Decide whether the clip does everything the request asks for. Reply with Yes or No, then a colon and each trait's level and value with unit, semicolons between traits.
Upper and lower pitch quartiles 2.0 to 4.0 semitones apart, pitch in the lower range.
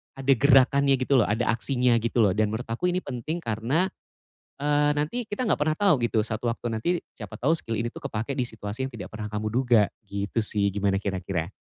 No: average, 4.5 semitones; low, 115 Hz